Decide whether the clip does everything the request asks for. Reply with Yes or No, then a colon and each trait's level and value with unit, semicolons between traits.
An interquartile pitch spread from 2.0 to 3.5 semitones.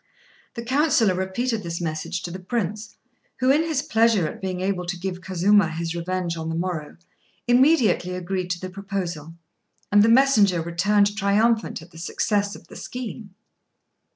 No: average, 4.3 semitones